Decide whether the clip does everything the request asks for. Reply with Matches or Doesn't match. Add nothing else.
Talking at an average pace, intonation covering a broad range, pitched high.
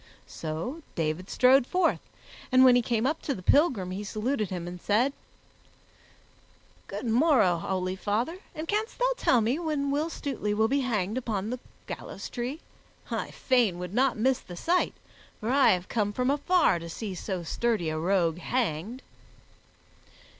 Matches